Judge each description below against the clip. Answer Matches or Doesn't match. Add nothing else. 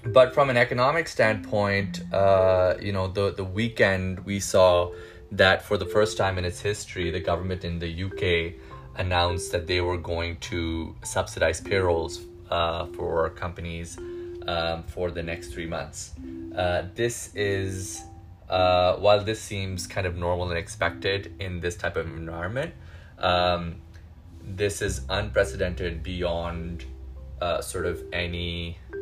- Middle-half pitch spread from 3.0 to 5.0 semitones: Doesn't match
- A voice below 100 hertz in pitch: Matches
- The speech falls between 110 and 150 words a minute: Matches